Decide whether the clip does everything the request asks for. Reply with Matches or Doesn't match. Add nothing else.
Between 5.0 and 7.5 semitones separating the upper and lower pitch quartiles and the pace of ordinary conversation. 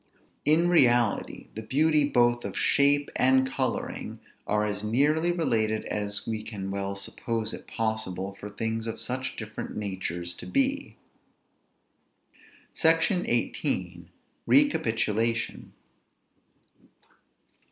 Doesn't match